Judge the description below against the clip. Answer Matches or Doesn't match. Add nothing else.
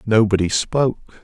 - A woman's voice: Doesn't match